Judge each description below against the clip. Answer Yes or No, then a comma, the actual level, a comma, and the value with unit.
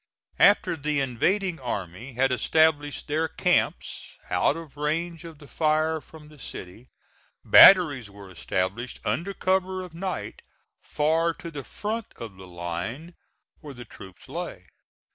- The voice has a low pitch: No, medium, 150 Hz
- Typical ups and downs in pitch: No, wide, 5.9 semitones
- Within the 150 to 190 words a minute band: No, average, 140 wpm